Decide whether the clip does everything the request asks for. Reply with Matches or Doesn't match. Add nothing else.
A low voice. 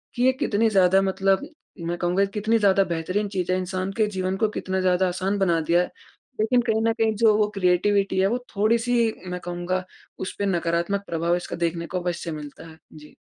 Doesn't match